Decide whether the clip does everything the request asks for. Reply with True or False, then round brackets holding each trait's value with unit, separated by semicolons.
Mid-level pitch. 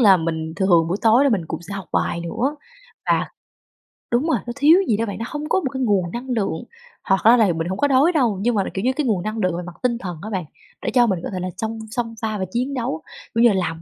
False (215 Hz)